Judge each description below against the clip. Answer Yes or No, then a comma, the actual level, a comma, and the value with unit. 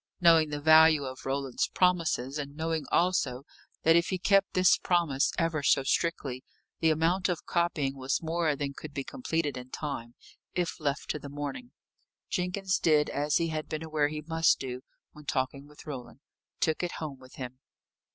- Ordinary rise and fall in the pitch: Yes, average, 3.2 semitones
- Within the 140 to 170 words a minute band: No, average, 180 wpm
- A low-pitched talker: No, medium, 155 Hz